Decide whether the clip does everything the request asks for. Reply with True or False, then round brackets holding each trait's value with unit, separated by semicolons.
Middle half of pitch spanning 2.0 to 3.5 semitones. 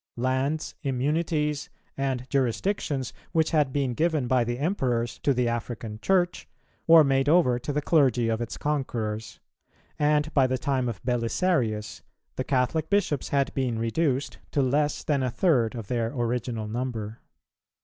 False (3.9 semitones)